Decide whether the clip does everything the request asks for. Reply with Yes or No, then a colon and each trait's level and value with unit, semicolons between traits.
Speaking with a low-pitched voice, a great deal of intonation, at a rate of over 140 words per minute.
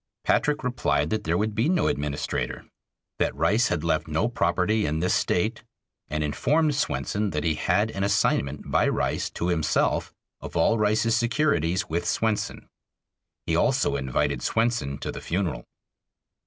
Yes: very low, 95 Hz; wide, 6.4 semitones; average, 155 wpm